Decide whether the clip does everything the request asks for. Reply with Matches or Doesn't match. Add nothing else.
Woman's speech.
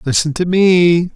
Doesn't match